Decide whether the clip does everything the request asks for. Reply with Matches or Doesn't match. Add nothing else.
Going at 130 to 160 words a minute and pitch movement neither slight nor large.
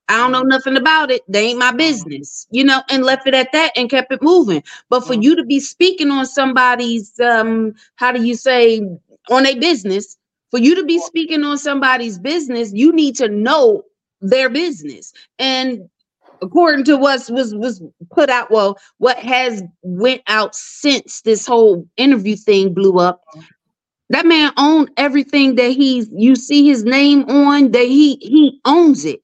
Doesn't match